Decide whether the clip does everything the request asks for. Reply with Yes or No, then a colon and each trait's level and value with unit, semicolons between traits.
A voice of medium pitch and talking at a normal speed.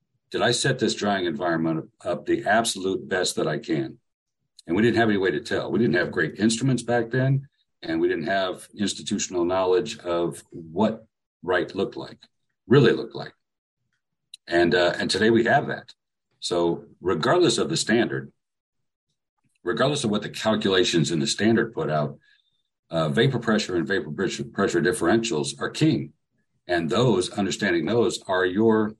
No: low, 110 Hz; average, 165 wpm